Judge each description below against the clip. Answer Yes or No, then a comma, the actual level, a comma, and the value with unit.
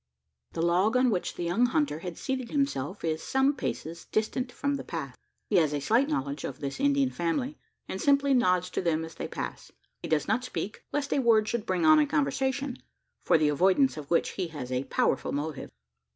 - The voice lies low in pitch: No, medium, 185 Hz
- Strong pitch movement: Yes, wide, 8.7 semitones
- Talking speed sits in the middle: No, fast, 210 wpm